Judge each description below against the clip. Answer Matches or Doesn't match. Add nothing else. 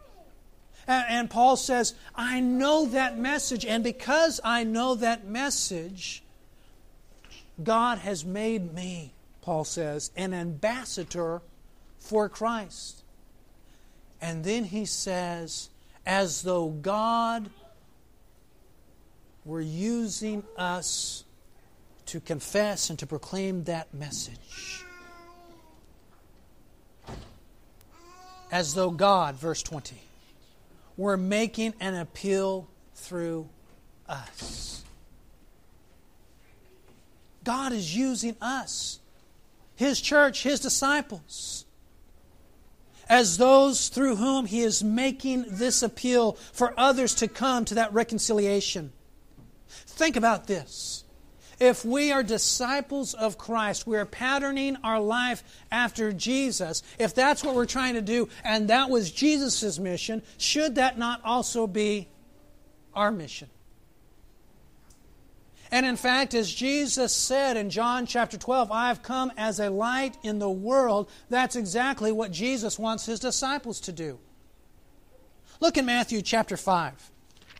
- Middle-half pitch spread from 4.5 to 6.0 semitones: Matches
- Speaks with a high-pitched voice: Matches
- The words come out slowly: Matches